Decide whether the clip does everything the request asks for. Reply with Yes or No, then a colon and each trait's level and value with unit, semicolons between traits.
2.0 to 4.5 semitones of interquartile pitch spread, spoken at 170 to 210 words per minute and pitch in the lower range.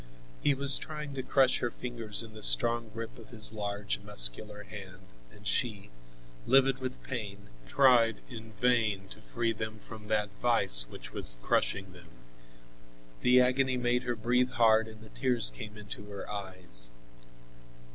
No: average, 3.2 semitones; average, 155 wpm; low, 110 Hz